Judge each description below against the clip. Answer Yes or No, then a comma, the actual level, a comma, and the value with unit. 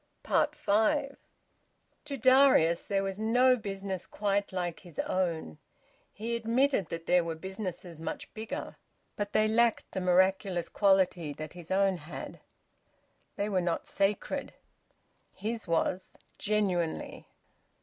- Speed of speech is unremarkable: No, slow, 120 wpm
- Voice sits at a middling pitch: No, high, 195 Hz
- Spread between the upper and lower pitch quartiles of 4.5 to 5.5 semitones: No, average, 3.7 semitones